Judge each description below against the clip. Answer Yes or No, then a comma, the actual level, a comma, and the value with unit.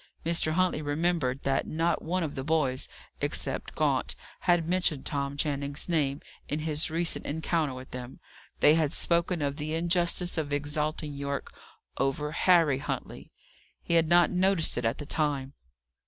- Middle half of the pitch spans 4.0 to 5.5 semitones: No, average, 3.1 semitones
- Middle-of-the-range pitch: Yes, medium, 155 Hz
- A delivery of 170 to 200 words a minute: No, average, 155 wpm